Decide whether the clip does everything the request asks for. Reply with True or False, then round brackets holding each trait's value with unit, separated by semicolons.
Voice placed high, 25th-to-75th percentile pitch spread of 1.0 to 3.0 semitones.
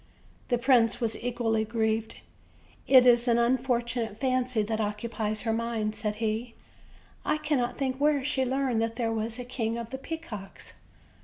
True (235 Hz; 2.4 semitones)